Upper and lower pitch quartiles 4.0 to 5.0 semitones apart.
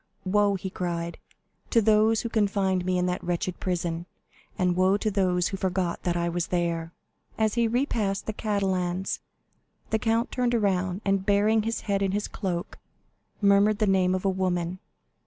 No: average, 2.7 semitones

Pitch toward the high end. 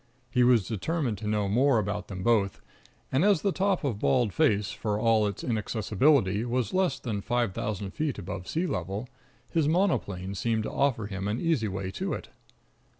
No: low, 110 Hz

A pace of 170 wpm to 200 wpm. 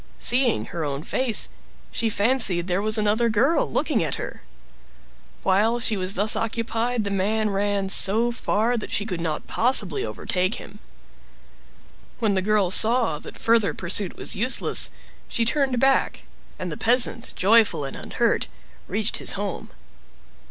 No: average, 150 wpm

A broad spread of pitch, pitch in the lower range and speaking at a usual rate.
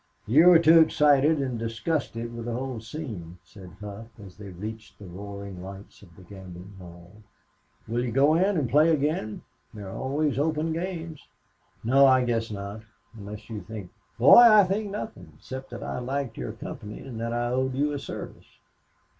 Yes: wide, 6.4 semitones; low, 120 Hz; average, 185 wpm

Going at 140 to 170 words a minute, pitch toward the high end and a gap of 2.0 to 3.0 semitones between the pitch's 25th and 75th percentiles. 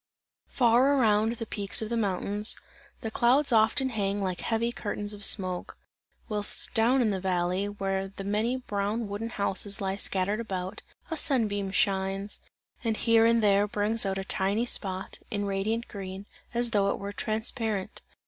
Yes: average, 165 wpm; high, 205 Hz; average, 2.7 semitones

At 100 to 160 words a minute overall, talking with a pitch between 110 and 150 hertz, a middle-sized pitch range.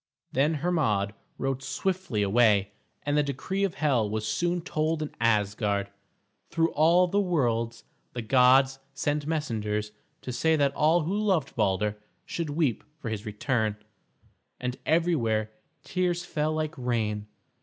No: average, 140 wpm; low, 135 Hz; wide, 6.9 semitones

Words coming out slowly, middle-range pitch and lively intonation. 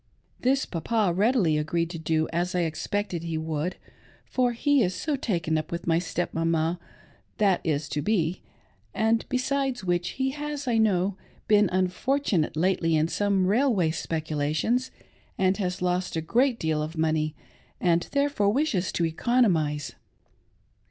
No: average, 160 wpm; medium, 180 Hz; wide, 5.9 semitones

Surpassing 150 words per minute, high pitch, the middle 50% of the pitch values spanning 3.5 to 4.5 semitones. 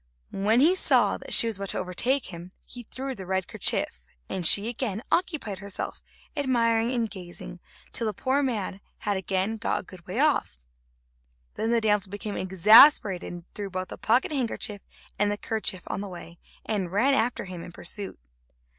Yes: average, 180 wpm; high, 205 Hz; average, 4.1 semitones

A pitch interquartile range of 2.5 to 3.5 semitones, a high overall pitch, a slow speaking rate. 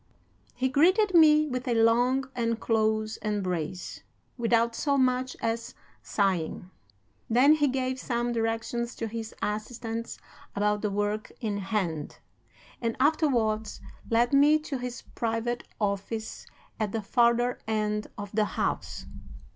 Yes: average, 3.0 semitones; high, 230 Hz; slow, 130 wpm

